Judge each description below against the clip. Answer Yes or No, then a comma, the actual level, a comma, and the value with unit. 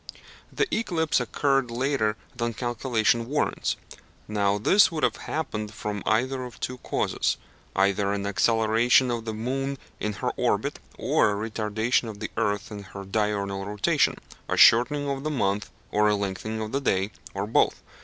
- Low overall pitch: Yes, low, 110 Hz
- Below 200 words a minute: Yes, average, 165 wpm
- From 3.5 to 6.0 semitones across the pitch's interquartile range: Yes, average, 3.8 semitones